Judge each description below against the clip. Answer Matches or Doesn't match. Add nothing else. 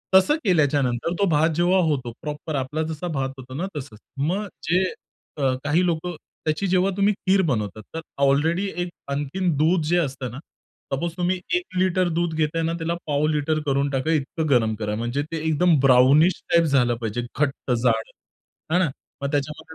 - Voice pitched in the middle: Matches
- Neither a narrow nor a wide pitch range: Matches